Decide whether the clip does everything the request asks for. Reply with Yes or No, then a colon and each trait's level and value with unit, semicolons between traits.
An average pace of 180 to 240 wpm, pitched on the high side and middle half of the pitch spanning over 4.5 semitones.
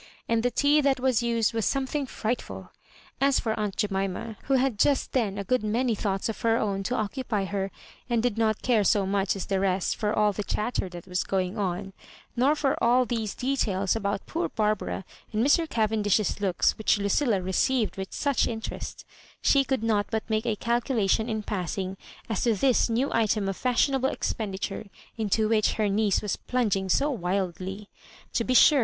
No: average, 190 wpm; high, 220 Hz; average, 3.7 semitones